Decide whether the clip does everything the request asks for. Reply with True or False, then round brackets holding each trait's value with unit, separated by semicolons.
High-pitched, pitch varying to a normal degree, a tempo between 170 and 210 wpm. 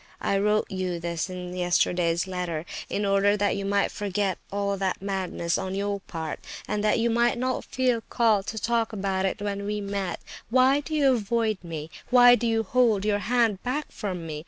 True (200 Hz; 3.4 semitones; 195 wpm)